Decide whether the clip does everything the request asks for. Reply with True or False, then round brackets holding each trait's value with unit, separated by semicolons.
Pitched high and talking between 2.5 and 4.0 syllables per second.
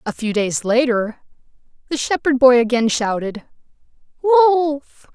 True (260 Hz; 3.9 syllables/s)